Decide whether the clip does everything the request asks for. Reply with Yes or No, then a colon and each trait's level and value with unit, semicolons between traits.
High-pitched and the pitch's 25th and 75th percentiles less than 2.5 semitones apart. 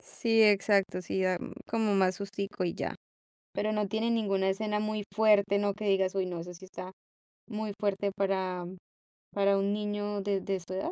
Yes: high, 200 Hz; narrow, 1.7 semitones